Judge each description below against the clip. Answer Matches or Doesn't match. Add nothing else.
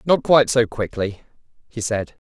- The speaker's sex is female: Doesn't match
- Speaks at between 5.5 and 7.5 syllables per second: Doesn't match